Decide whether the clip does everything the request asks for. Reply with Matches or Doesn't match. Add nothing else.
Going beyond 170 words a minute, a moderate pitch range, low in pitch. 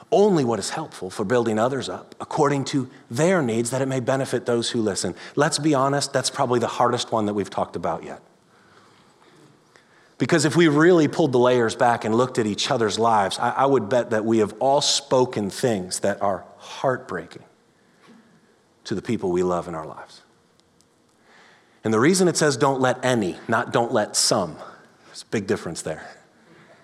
Matches